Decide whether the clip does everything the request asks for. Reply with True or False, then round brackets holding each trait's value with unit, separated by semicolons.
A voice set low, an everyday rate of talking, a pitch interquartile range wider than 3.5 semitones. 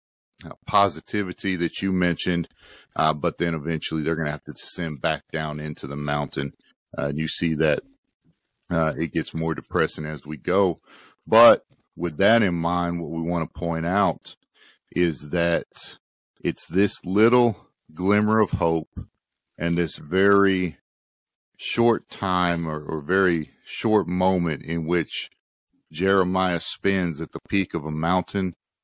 False (85 Hz; 150 wpm; 3.1 semitones)